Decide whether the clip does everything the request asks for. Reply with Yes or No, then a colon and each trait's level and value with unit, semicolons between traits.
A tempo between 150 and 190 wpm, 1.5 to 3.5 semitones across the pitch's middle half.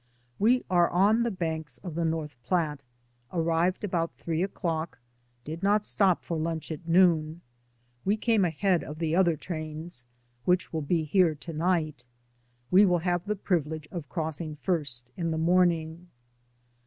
Yes: average, 155 wpm; narrow, 2.5 semitones